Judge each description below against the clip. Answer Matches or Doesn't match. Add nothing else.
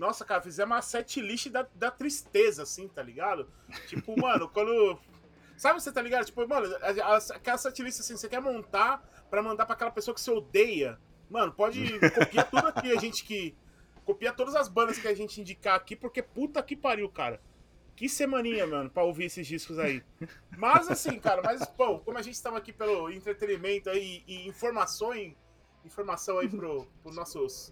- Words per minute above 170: Matches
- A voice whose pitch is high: Matches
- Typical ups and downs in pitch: Matches